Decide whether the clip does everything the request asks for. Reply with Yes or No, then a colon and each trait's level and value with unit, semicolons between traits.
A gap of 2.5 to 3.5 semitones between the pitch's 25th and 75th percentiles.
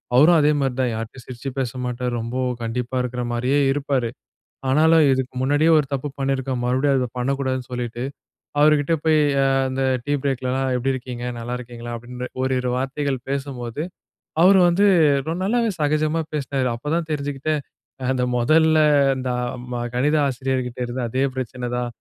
Yes: average, 2.8 semitones